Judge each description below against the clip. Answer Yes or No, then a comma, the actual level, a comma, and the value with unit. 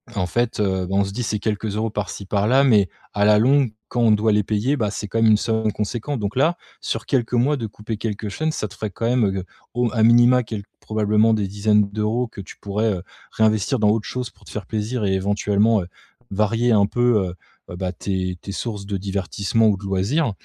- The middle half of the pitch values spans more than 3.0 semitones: No, narrow, 2.5 semitones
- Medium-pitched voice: No, low, 105 Hz